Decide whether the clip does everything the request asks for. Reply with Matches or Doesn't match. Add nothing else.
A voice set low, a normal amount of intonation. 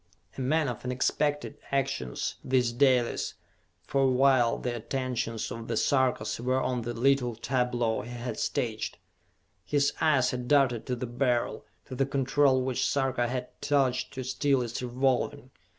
Doesn't match